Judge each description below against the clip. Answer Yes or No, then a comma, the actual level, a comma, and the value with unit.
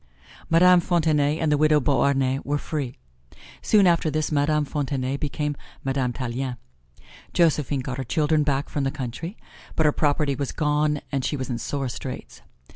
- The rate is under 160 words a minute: No, average, 165 wpm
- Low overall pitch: No, medium, 145 Hz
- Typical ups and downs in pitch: No, narrow, 2.3 semitones